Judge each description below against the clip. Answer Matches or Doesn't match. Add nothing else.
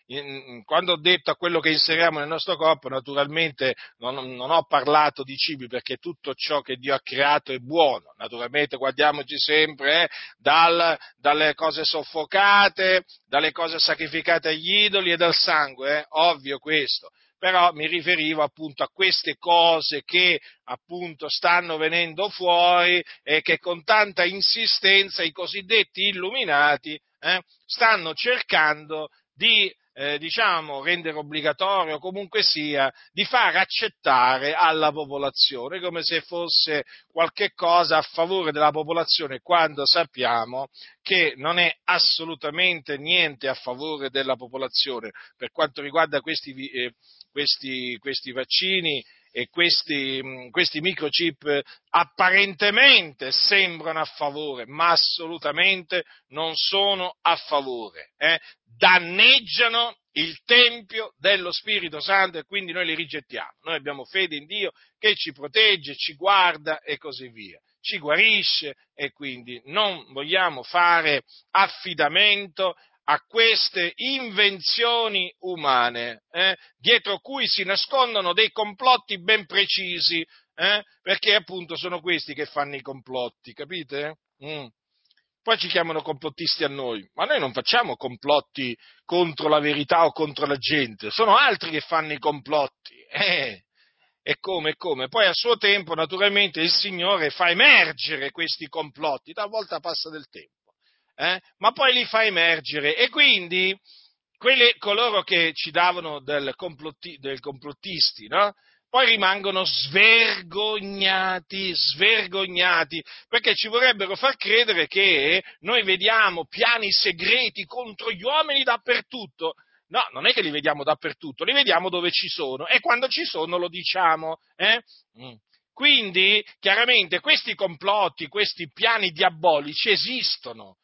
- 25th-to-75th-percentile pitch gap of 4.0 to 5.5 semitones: Matches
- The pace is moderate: Matches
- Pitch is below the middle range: Doesn't match